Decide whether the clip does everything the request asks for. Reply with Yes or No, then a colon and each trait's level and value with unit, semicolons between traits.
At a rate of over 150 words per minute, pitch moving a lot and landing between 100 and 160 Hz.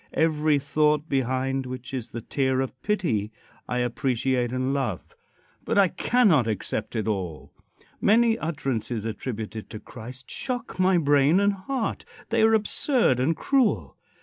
No: average, 145 wpm; wide, 7.1 semitones; low, 135 Hz